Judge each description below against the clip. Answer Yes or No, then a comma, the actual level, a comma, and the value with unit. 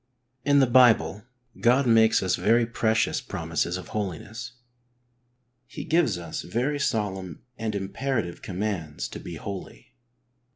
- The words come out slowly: Yes, slow, 130 wpm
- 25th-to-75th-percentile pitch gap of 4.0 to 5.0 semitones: Yes, average, 4.4 semitones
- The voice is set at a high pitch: No, low, 110 Hz